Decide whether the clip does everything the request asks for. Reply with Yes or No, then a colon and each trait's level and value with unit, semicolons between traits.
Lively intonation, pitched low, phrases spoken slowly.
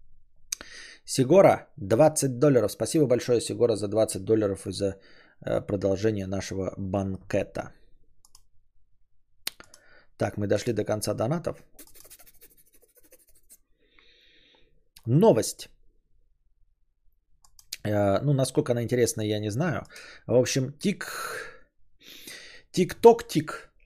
Yes: wide, 7.3 semitones; low, 105 Hz; slow, 80 wpm